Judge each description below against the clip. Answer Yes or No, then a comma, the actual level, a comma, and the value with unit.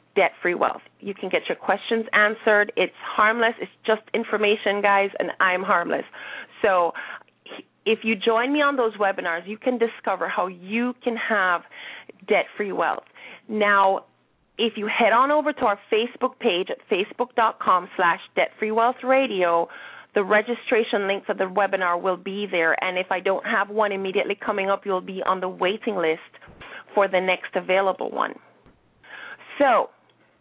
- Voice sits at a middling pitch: No, high, 205 Hz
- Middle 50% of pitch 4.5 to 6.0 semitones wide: No, average, 3.1 semitones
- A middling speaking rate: Yes, average, 165 wpm